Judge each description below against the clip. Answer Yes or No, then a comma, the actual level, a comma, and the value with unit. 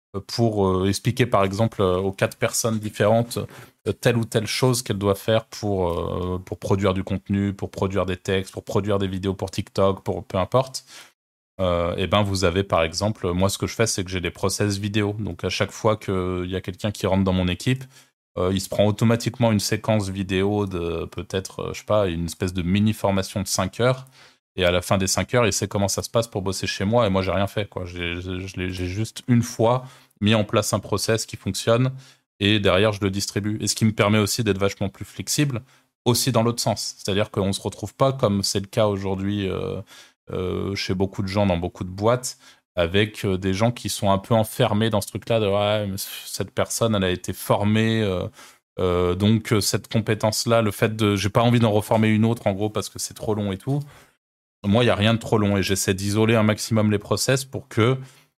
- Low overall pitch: Yes, low, 105 Hz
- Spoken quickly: Yes, fast, 235 wpm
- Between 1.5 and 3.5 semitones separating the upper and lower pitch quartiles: Yes, average, 2.8 semitones